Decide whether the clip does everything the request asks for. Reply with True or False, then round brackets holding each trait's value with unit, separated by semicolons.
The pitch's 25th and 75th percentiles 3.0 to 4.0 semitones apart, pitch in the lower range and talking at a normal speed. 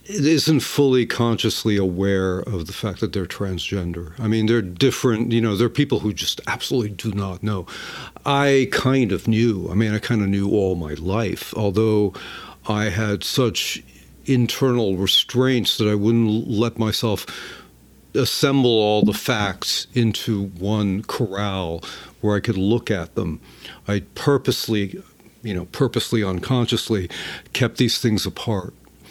True (3.3 semitones; 110 Hz; 150 wpm)